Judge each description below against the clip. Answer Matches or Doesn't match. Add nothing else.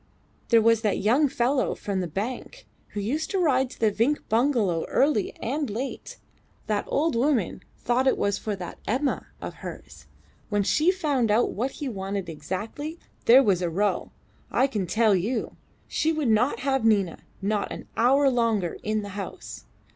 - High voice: Matches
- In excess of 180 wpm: Doesn't match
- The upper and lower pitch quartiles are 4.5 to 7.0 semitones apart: Matches